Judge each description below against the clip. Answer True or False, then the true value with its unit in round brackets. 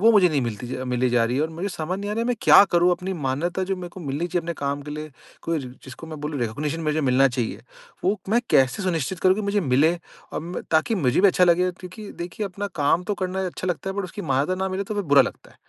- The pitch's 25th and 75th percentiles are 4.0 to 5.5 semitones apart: True (4.9 semitones)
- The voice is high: False (170 Hz)